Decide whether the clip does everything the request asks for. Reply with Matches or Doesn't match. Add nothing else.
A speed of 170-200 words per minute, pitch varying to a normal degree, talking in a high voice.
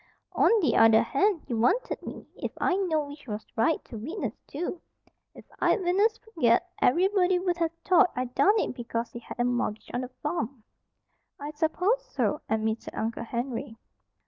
Doesn't match